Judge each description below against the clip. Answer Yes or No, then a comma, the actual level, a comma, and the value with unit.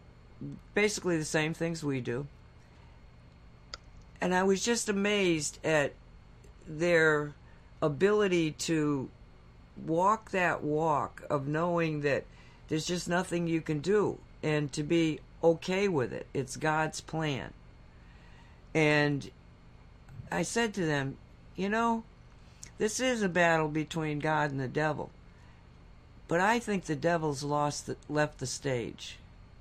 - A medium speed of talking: No, slow, 125 wpm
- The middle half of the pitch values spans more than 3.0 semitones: Yes, average, 4.6 semitones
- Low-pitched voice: No, medium, 155 Hz